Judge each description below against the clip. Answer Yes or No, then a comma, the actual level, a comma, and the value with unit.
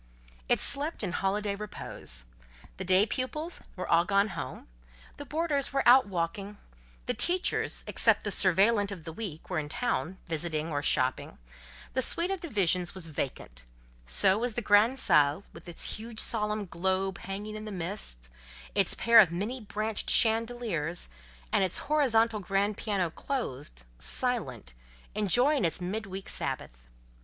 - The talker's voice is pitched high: Yes, high, 200 Hz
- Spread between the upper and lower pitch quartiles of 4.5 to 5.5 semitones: Yes, average, 5.2 semitones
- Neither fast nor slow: Yes, average, 150 wpm